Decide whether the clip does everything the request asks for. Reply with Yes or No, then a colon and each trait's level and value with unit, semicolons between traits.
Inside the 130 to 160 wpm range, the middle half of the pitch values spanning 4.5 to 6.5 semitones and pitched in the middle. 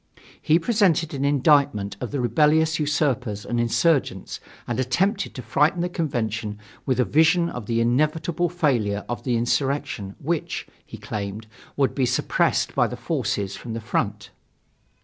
No: average, 150 wpm; wide, 5.5 semitones; low, 130 Hz